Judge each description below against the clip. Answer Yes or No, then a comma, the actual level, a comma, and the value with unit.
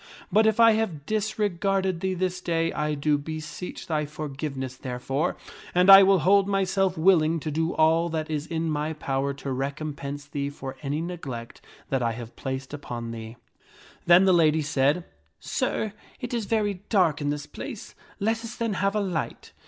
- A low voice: No, medium, 160 Hz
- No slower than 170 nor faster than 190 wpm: Yes, average, 180 wpm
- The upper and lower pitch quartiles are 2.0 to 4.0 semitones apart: No, average, 5.1 semitones